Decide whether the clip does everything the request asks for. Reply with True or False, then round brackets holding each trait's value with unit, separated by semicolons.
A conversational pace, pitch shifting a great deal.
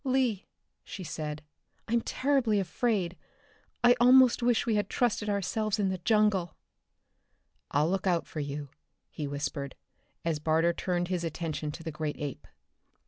True (145 wpm; 5.9 semitones)